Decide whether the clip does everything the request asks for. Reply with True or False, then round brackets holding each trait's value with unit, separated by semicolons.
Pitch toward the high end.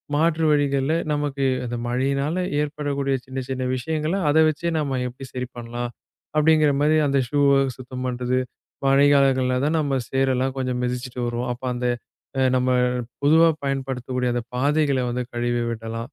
False (135 Hz)